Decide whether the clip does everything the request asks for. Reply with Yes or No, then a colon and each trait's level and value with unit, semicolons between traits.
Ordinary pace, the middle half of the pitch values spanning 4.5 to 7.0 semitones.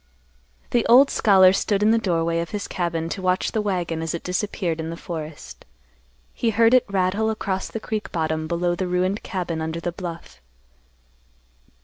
No: average, 175 wpm; average, 3.8 semitones